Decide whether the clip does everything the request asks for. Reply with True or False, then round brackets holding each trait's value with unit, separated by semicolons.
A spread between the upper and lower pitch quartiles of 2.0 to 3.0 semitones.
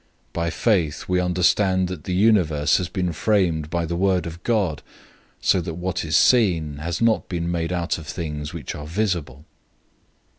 True (2.7 semitones)